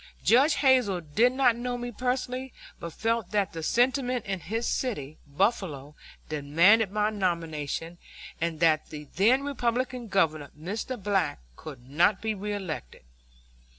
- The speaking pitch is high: Yes, high, 205 Hz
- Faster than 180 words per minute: No, slow, 135 wpm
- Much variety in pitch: Yes, wide, 6.9 semitones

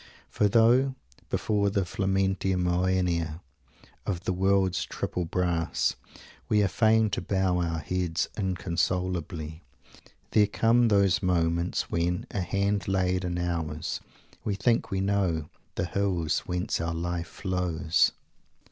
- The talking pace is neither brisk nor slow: No, slow, 125 wpm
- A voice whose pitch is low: Yes, very low, 90 Hz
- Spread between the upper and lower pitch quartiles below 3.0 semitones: Yes, narrow, 2.5 semitones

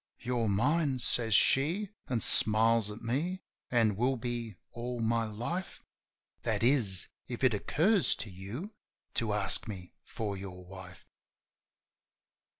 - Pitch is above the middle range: No, low, 115 Hz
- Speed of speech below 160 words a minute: Yes, slow, 135 wpm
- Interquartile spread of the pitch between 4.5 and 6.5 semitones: No, average, 3.9 semitones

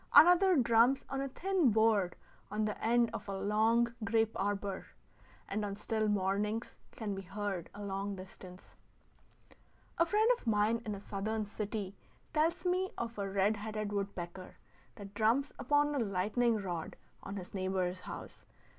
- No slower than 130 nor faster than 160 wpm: Yes, average, 155 wpm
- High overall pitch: Yes, high, 210 Hz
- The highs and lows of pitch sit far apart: No, average, 3.0 semitones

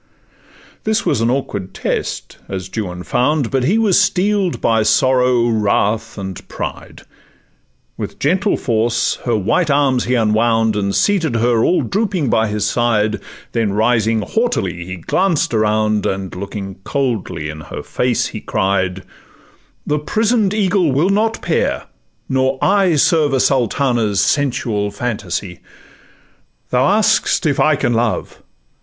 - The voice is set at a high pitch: No, low, 120 Hz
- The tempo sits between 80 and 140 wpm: Yes, slow, 135 wpm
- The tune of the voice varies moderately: No, wide, 5.9 semitones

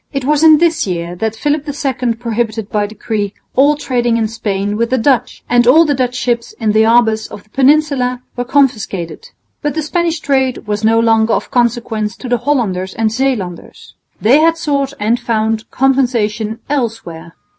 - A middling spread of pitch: Yes, average, 4.0 semitones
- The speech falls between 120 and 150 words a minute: No, average, 175 wpm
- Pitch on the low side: No, high, 240 Hz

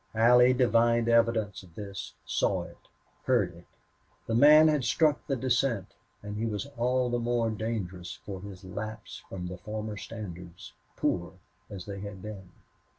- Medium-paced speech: Yes, average, 155 wpm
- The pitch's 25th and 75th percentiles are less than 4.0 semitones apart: Yes, average, 3.6 semitones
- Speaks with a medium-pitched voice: No, low, 110 Hz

